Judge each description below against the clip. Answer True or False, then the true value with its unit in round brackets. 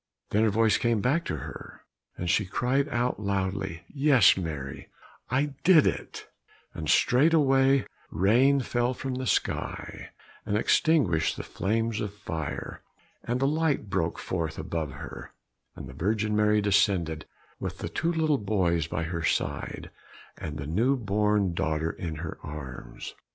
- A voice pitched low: True (105 Hz)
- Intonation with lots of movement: True (7.4 semitones)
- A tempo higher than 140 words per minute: True (150 wpm)